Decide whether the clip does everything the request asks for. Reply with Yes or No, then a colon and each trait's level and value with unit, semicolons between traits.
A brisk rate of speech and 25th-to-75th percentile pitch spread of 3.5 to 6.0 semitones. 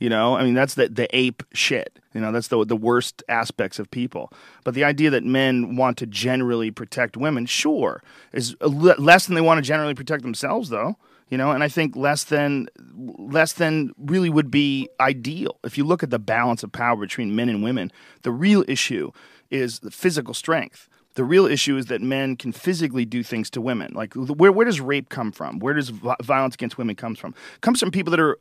Yes: fast, 220 wpm; average, 4.2 semitones